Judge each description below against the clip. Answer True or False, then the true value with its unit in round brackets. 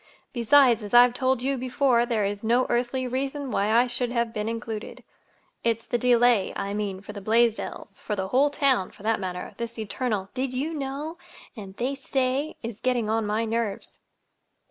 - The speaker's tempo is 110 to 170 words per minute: False (180 wpm)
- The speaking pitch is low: False (235 Hz)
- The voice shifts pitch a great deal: False (3.2 semitones)